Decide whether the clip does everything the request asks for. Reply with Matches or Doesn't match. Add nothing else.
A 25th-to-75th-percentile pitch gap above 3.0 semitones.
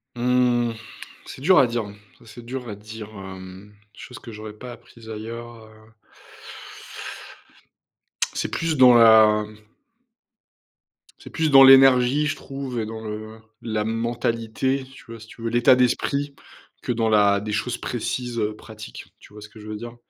Doesn't match